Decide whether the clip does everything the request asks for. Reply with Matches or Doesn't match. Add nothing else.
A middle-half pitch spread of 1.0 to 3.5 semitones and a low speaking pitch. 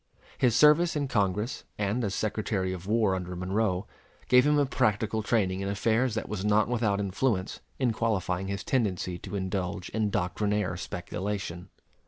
Matches